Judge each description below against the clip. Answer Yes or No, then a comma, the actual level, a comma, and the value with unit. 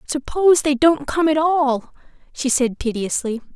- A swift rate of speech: No, average, 150 wpm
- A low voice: No, very high, 280 Hz